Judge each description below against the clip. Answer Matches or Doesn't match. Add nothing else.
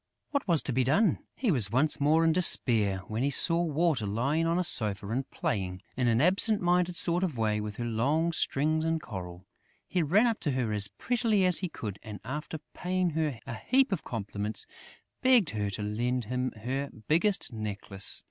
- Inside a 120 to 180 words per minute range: Doesn't match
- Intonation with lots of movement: Matches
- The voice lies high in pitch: Doesn't match